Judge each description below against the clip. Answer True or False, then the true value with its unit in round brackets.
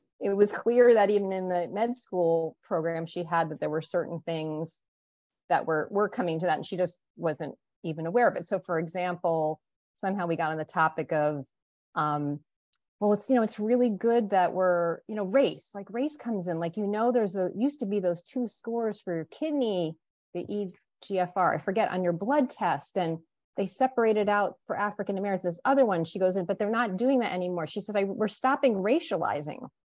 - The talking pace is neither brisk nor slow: False (210 wpm)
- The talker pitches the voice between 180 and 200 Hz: True (190 Hz)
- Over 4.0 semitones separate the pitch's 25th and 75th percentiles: True (4.6 semitones)